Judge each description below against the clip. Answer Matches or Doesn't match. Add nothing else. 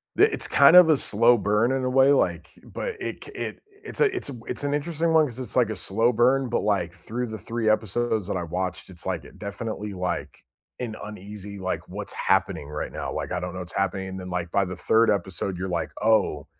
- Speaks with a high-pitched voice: Doesn't match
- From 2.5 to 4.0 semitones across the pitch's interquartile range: Doesn't match